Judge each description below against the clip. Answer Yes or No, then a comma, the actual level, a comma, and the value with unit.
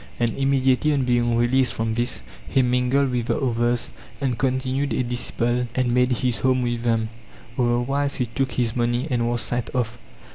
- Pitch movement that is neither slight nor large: No, narrow, 1.6 semitones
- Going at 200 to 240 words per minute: No, average, 190 wpm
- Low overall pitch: Yes, low, 125 Hz